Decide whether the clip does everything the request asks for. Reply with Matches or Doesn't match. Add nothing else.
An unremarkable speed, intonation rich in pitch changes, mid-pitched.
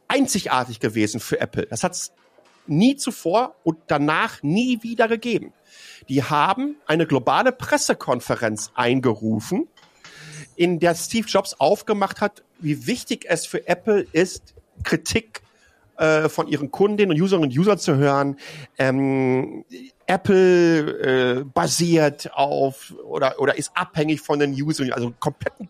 Matches